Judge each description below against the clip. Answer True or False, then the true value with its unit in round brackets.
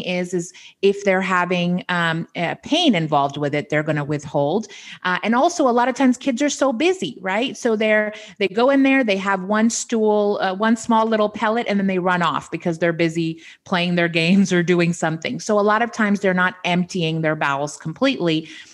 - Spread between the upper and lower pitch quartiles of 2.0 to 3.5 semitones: False (4.6 semitones)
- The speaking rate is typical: False (215 wpm)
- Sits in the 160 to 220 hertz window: True (190 Hz)